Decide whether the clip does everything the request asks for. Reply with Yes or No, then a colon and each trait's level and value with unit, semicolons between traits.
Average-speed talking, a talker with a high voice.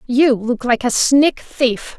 Yes: average, 180 wpm; very high, 250 Hz